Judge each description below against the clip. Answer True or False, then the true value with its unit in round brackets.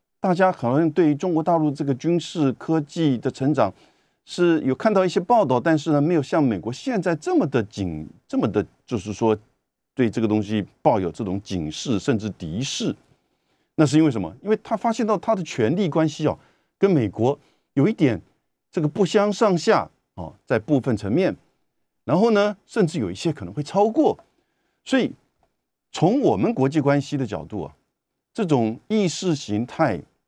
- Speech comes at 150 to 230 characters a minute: False (265 characters per minute)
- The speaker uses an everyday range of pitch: False (7.5 semitones)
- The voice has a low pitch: False (155 Hz)